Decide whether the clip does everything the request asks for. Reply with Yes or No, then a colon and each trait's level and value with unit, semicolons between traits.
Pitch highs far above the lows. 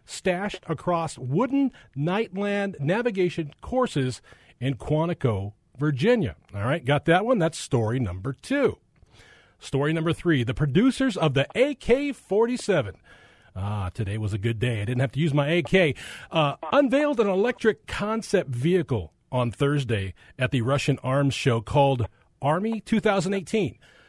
Yes: wide, 7.7 semitones